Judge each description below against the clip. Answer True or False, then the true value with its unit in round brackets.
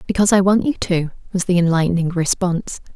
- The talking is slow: False (180 wpm)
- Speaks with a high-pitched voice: False (180 Hz)